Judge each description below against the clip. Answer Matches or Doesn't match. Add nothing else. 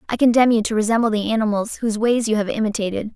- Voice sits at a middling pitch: Doesn't match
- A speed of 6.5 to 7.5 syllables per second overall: Matches